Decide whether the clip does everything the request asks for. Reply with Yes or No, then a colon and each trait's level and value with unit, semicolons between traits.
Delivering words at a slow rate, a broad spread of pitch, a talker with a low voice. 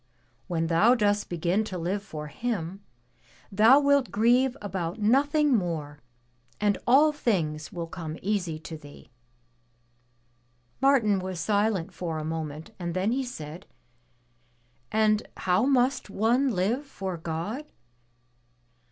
No: slow, 125 wpm; wide, 6.4 semitones; high, 200 Hz